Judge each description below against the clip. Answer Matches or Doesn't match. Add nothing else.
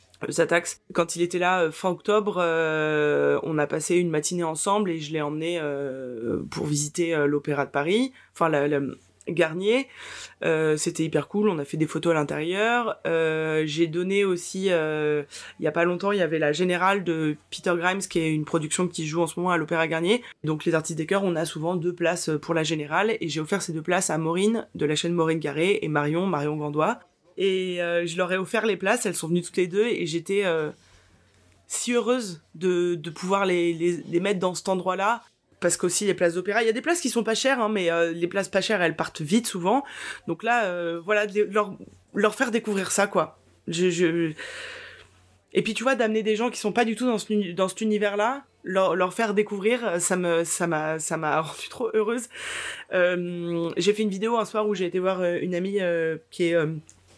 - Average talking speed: Doesn't match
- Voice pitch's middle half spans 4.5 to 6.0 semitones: Doesn't match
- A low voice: Doesn't match